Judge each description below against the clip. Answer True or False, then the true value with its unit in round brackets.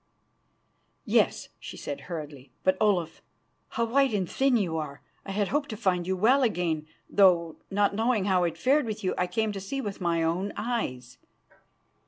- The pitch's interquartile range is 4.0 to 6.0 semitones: True (4.7 semitones)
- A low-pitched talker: False (195 Hz)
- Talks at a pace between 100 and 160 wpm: False (180 wpm)